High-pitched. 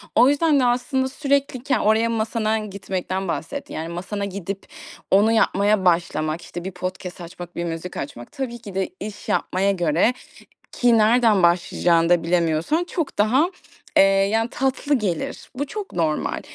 Yes: high, 200 Hz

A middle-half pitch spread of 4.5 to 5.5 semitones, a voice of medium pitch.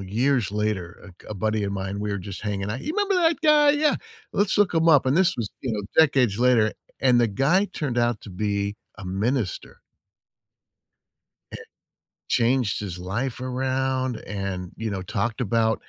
No: average, 4.9 semitones; low, 115 Hz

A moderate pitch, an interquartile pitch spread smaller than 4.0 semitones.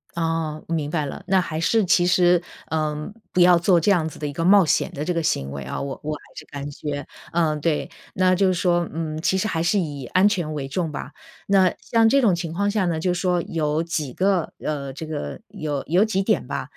Yes: medium, 165 Hz; average, 3.3 semitones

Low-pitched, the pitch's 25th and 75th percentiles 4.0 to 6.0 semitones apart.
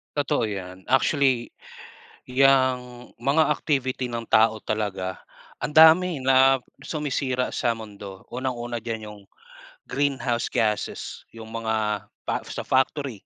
No: low, 125 Hz; average, 3.5 semitones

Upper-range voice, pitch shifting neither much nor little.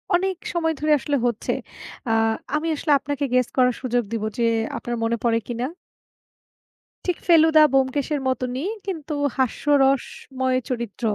Yes: very high, 265 Hz; average, 3.6 semitones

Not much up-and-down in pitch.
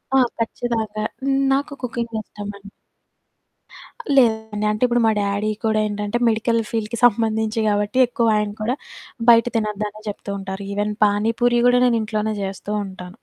Yes: narrow, 1.9 semitones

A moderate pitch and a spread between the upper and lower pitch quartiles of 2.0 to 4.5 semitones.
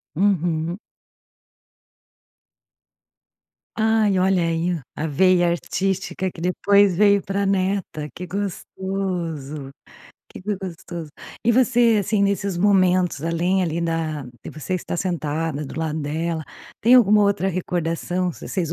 Yes: medium, 180 Hz; average, 3.2 semitones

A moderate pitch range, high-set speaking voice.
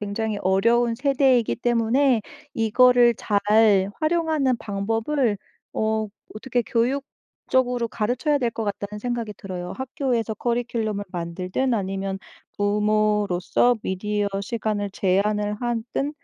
Yes: average, 3.2 semitones; high, 225 Hz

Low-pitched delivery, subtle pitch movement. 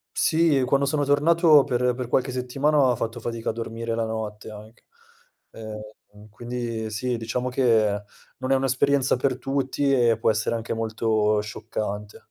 No: low, 120 Hz; average, 3.4 semitones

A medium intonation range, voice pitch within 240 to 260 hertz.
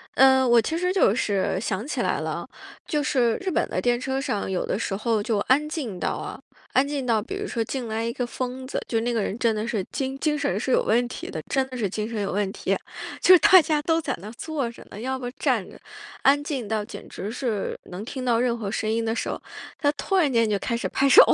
Yes: average, 4.1 semitones; high, 245 Hz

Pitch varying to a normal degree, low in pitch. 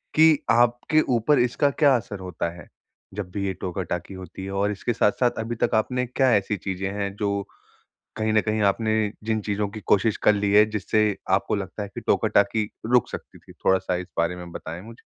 Yes: average, 3.0 semitones; low, 105 Hz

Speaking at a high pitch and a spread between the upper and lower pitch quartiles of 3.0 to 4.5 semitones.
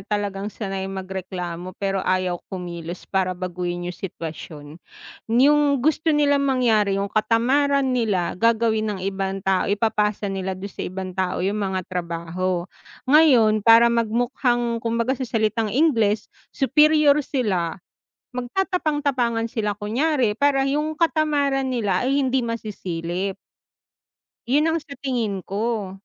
No: high, 215 Hz; wide, 5.6 semitones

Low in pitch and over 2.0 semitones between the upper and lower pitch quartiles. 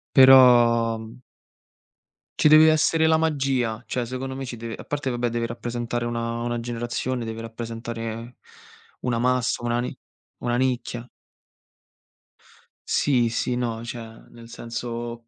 No: low, 120 Hz; narrow, 1.5 semitones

